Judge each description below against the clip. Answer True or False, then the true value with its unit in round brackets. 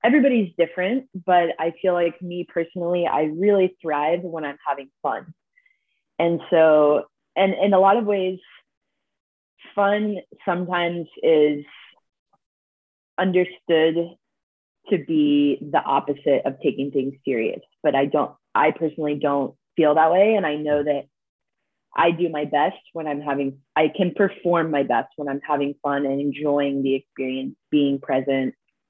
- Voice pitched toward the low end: False (160 Hz)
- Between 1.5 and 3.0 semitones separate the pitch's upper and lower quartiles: False (4.1 semitones)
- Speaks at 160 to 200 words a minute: False (145 wpm)